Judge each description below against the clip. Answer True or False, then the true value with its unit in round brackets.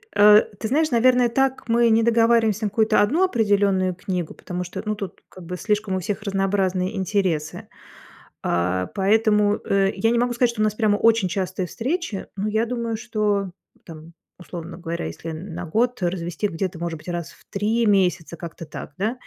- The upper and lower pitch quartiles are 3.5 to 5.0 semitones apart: True (3.9 semitones)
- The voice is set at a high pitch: True (205 Hz)